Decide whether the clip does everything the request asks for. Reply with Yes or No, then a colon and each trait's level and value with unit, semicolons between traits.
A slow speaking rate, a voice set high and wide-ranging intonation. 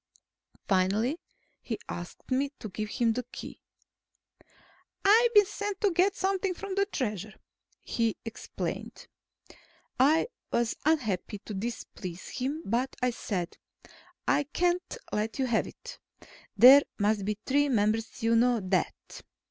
Yes: slow, 130 wpm; high, 240 Hz; wide, 7.4 semitones